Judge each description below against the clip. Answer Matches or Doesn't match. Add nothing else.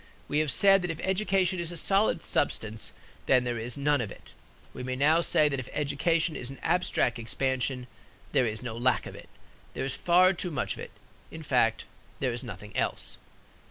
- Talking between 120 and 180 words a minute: Doesn't match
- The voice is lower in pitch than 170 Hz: Matches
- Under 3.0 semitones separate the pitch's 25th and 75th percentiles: Doesn't match